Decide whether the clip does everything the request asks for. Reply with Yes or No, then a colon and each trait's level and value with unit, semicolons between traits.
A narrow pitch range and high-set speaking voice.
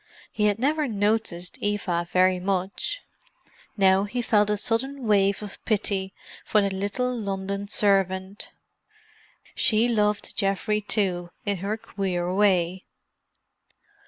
Yes: narrow, 1.9 semitones; high, 200 Hz